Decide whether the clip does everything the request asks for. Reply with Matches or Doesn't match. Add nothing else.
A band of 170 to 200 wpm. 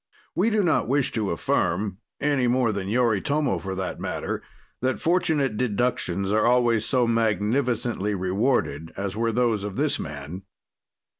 Doesn't match